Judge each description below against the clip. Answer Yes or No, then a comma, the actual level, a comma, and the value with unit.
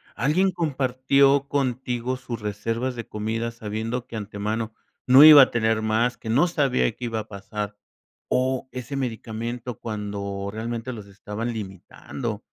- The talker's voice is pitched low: Yes, low, 115 Hz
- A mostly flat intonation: No, average, 3.0 semitones